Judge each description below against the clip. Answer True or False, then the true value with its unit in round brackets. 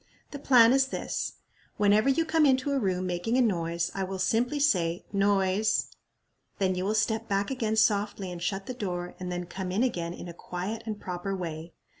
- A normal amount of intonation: True (4.1 semitones)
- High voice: True (200 Hz)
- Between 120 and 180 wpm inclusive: False (200 wpm)